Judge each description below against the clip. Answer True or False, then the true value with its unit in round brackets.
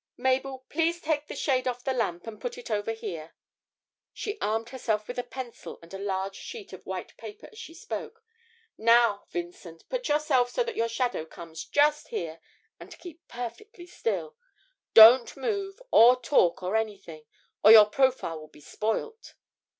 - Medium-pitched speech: False (245 Hz)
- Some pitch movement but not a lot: False (7.7 semitones)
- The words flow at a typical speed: True (170 wpm)